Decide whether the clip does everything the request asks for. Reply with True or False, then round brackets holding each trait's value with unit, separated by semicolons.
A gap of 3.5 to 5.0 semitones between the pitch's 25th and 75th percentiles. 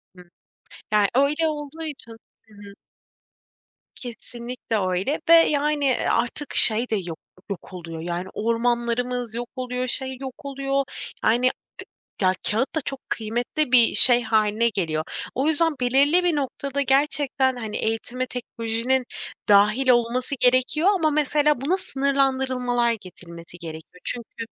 True (3.8 semitones)